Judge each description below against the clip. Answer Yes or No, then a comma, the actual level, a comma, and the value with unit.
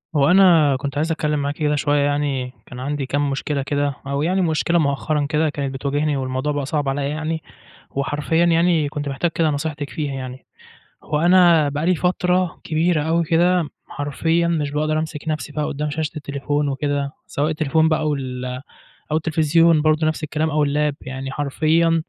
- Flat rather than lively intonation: Yes, narrow, 2.1 semitones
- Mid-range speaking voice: Yes, medium, 150 Hz